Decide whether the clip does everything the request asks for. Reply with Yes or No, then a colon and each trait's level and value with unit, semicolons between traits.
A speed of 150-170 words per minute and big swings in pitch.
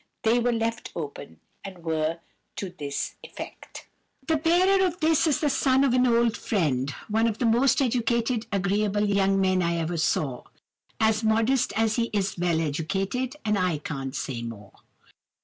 Yes: average, 165 wpm; wide, 6.3 semitones